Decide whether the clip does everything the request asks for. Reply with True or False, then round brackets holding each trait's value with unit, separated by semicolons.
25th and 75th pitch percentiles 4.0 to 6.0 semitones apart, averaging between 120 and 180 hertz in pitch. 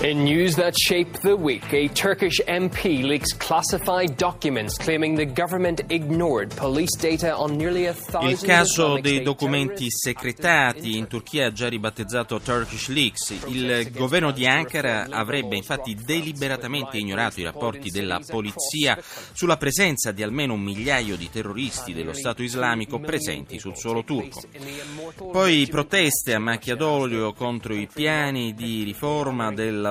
True (5.5 semitones; 135 Hz)